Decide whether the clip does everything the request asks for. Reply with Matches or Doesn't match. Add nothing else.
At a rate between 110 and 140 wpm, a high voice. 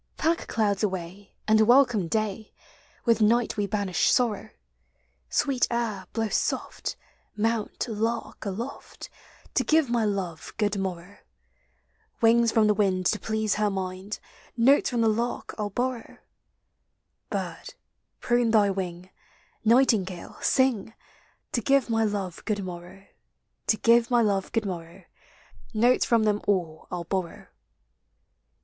Matches